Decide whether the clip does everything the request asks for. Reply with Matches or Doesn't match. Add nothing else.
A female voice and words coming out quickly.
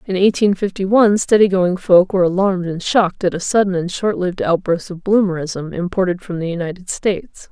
Doesn't match